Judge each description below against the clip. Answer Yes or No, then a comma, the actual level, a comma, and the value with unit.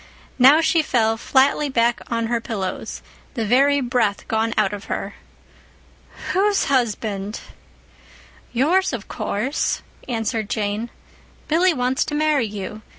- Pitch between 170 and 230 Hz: No, high, 240 Hz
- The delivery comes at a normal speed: No, slow, 125 wpm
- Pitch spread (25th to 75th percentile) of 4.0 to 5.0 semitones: Yes, average, 4.6 semitones